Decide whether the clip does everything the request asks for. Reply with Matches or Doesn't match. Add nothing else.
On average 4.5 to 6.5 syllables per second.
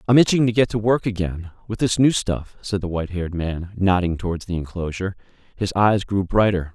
Matches